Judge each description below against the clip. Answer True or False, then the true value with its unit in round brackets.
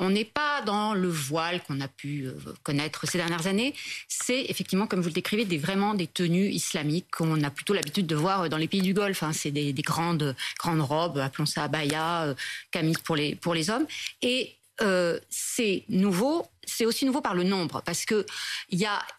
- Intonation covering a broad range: False (4.4 semitones)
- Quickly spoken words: False (205 wpm)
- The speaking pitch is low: False (175 Hz)